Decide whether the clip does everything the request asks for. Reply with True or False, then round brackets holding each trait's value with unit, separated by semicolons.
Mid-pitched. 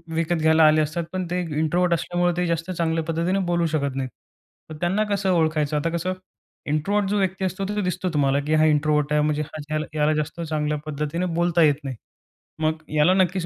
True (160 Hz)